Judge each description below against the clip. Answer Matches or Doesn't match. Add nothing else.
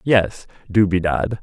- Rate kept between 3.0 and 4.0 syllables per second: Matches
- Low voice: Matches